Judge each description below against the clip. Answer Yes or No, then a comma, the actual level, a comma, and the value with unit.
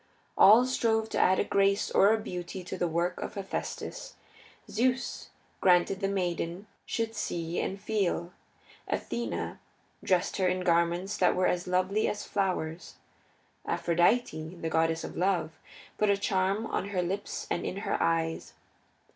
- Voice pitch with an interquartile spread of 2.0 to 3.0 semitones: Yes, average, 2.7 semitones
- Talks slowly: No, average, 155 wpm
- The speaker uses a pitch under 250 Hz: Yes, medium, 185 Hz